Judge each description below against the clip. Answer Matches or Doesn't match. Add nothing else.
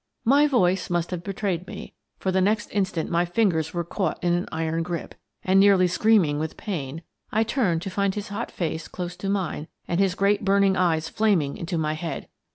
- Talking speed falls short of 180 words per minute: Doesn't match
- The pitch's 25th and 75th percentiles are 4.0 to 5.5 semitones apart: Doesn't match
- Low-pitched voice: Doesn't match